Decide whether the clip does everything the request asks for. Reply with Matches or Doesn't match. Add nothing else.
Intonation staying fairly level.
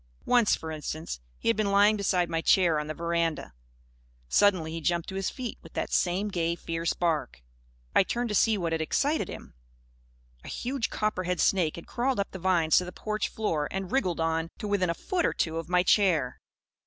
Doesn't match